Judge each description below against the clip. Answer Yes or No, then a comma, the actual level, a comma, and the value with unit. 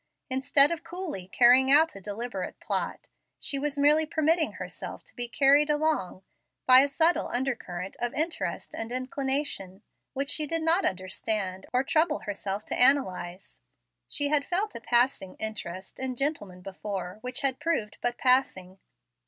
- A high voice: Yes, very high, 255 Hz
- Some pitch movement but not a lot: No, wide, 6.7 semitones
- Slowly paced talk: No, average, 155 wpm